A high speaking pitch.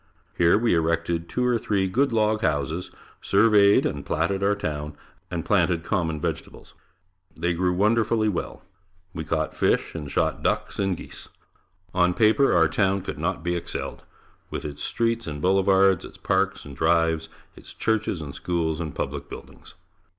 No: very low, 90 Hz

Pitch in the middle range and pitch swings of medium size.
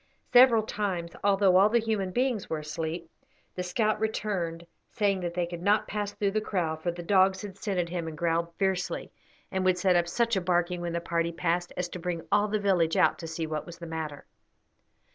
Yes: medium, 180 Hz; average, 3.2 semitones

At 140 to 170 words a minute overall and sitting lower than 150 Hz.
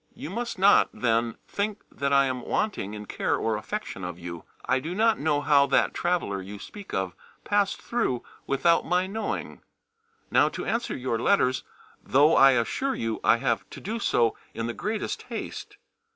No: average, 180 wpm; medium, 140 Hz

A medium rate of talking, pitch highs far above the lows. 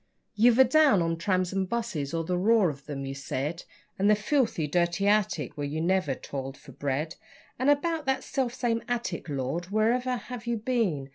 Yes: average, 195 wpm; wide, 7.7 semitones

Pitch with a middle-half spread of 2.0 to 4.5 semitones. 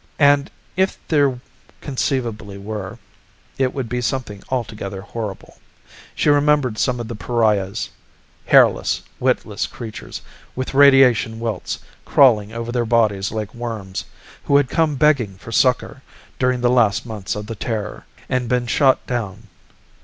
Yes: average, 3.5 semitones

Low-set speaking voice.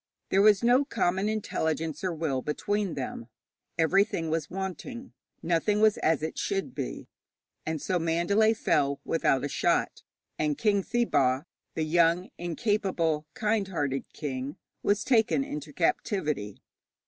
No: medium, 170 Hz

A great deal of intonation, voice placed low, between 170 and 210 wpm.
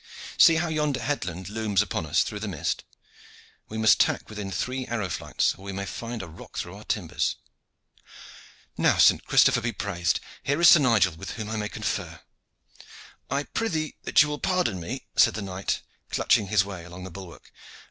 Yes: wide, 5.8 semitones; low, 105 Hz; average, 190 wpm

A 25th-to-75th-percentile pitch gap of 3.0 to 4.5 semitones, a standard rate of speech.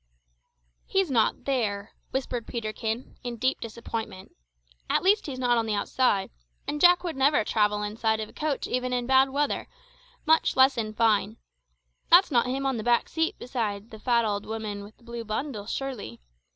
Yes: average, 3.7 semitones; average, 180 wpm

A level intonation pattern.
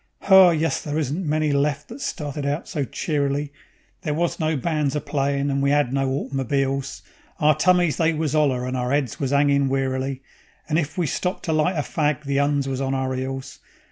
Yes: narrow, 2.2 semitones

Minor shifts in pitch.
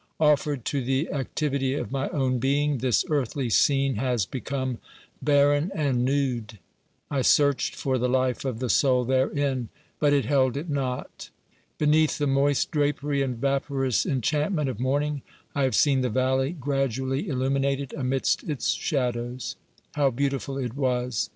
Yes: narrow, 2.0 semitones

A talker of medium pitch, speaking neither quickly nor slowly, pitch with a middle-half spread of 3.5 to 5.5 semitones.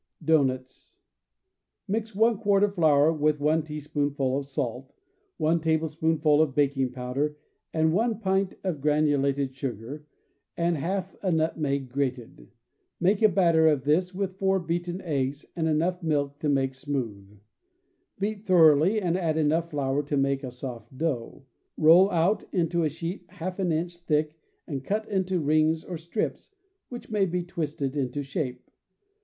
Yes: medium, 155 Hz; average, 155 wpm; average, 4.1 semitones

